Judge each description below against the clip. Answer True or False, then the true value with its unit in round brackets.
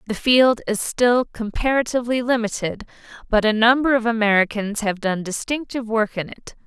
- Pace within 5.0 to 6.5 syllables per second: True (5.3 syllables/s)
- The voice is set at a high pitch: True (225 Hz)